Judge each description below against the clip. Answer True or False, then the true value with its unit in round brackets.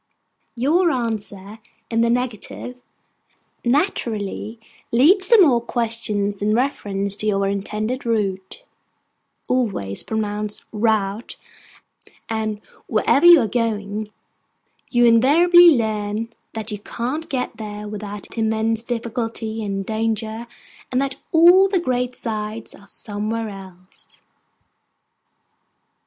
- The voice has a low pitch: False (225 Hz)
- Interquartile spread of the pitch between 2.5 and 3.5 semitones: True (3.2 semitones)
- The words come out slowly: True (105 wpm)